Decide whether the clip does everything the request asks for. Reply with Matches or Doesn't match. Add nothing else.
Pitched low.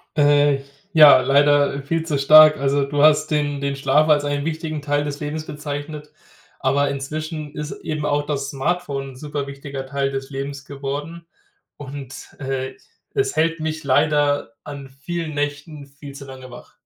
Doesn't match